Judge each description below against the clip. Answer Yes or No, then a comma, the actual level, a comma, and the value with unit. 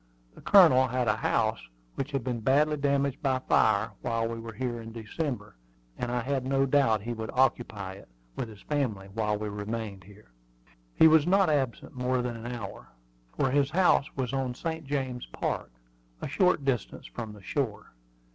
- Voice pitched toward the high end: No, low, 125 Hz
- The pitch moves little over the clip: No, average, 3.8 semitones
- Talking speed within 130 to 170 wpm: No, average, 185 wpm